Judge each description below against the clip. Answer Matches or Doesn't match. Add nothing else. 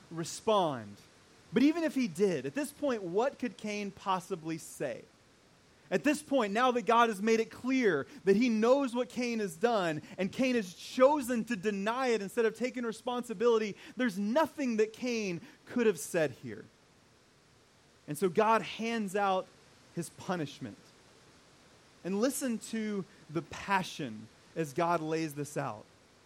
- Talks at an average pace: Matches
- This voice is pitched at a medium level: Doesn't match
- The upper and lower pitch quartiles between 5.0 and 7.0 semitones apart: Matches